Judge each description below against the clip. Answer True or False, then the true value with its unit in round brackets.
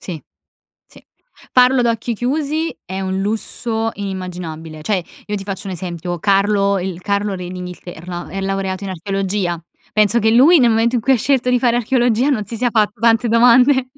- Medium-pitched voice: False (205 Hz)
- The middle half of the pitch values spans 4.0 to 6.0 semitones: True (4.3 semitones)